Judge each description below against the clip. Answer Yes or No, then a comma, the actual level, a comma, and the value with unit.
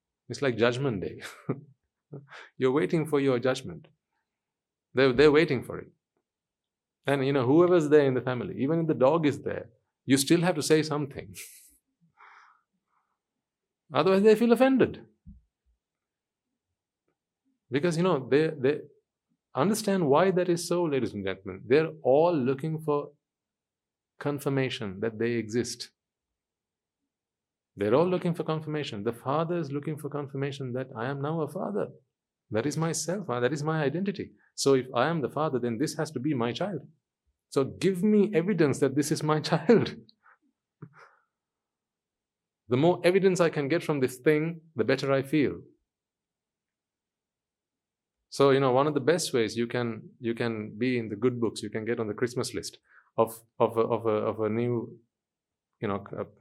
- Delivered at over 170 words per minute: No, average, 165 wpm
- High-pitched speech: No, medium, 140 Hz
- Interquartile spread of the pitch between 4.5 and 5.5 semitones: Yes, average, 5.0 semitones